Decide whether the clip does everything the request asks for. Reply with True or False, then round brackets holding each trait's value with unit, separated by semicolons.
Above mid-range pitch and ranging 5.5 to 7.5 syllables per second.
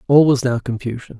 False (125 Hz; 5.9 syllables/s)